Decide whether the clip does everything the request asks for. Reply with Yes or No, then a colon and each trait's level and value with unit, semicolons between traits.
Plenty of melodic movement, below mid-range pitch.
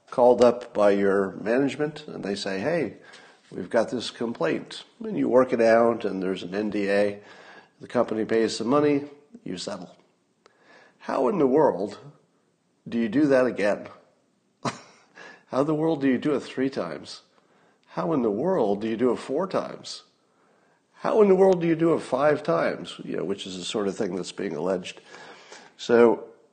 Yes: wide, 5.9 semitones; low, 120 Hz